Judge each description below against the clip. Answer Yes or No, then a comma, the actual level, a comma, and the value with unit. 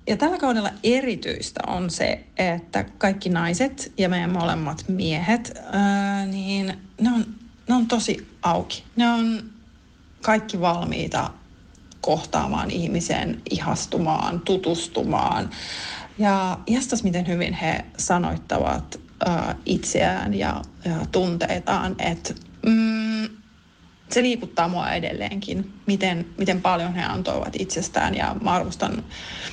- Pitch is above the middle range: Yes, high, 195 Hz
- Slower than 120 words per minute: Yes, average, 110 wpm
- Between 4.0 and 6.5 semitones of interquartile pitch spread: Yes, average, 4.3 semitones